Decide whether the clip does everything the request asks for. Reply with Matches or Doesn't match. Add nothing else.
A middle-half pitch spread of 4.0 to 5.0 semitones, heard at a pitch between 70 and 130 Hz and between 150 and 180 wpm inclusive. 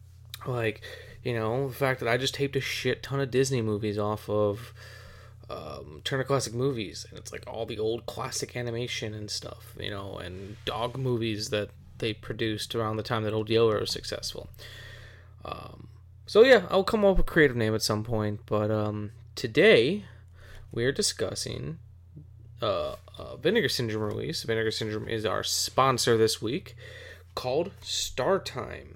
Doesn't match